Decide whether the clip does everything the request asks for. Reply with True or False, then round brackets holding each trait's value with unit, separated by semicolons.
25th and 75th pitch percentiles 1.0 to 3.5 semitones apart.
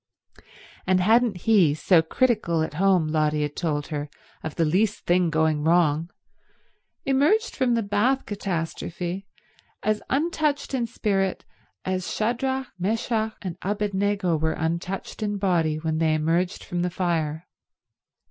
False (5.1 semitones)